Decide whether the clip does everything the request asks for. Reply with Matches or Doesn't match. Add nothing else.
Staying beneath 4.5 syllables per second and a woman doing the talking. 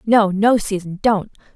Matches